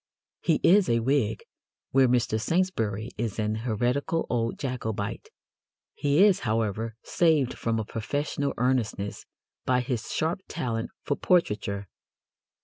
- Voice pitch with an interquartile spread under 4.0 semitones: No, average, 4.6 semitones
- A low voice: Yes, low, 120 Hz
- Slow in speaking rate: Yes, slow, 125 wpm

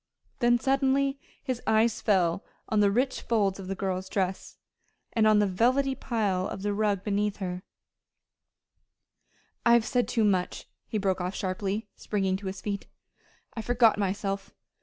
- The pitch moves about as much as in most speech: Yes, average, 3.4 semitones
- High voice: Yes, high, 205 Hz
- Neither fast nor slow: Yes, average, 160 wpm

